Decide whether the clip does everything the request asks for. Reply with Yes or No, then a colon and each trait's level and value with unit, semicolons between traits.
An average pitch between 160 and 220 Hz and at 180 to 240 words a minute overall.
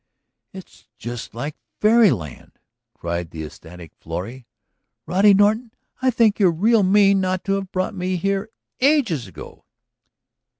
No: medium, 185 Hz; slow, 135 wpm